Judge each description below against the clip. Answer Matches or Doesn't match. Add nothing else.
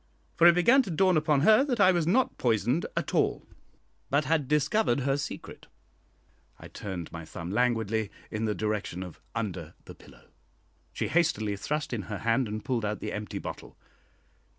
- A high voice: Doesn't match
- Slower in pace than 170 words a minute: Doesn't match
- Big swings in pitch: Matches